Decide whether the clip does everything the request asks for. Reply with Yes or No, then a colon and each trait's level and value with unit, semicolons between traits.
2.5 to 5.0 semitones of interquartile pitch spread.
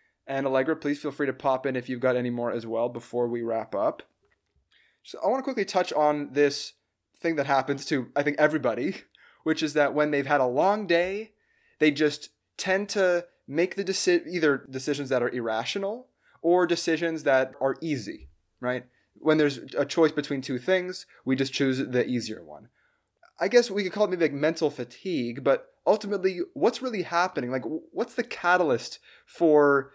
No: wide, 5.4 semitones